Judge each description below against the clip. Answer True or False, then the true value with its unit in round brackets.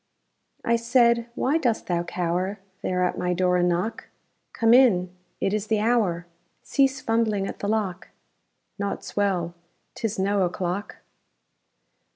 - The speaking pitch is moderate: False (200 Hz)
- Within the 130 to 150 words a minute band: True (140 wpm)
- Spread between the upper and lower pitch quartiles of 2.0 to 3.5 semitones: False (4.2 semitones)